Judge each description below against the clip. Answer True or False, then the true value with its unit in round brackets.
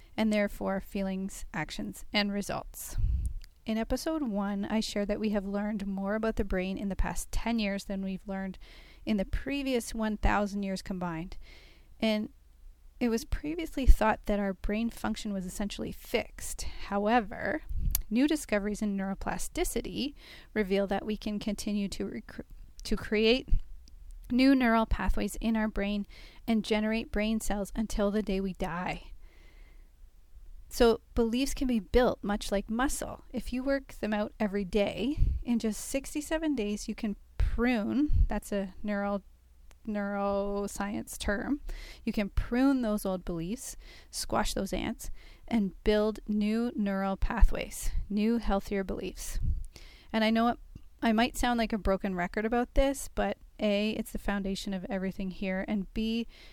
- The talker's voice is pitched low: False (210 Hz)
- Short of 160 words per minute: True (150 wpm)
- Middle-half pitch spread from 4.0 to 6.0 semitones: False (2.6 semitones)